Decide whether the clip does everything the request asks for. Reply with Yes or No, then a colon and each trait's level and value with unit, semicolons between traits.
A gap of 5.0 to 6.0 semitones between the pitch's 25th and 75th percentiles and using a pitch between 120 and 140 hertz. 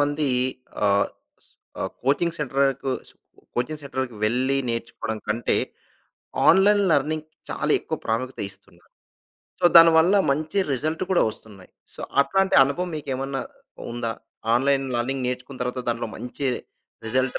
No: average, 4.2 semitones; low, 135 Hz